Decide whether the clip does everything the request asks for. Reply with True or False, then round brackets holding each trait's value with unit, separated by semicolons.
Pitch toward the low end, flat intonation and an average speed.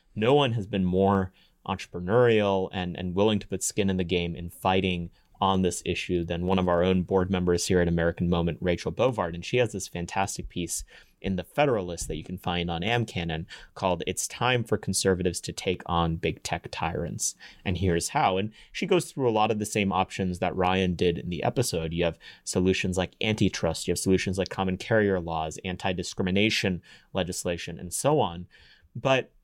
True (90 Hz; 2.1 semitones; 195 wpm)